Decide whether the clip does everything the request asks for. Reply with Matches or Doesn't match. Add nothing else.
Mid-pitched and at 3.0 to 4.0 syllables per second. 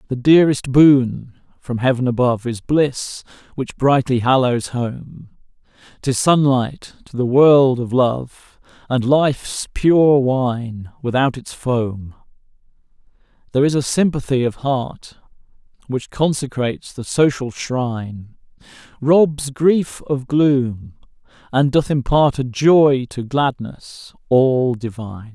Doesn't match